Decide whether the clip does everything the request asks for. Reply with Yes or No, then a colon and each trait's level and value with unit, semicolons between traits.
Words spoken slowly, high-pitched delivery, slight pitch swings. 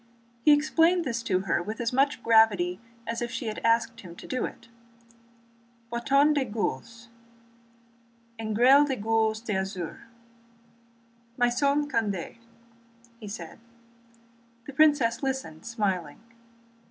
Yes: slow, 115 wpm; high, 230 Hz; narrow, 2.3 semitones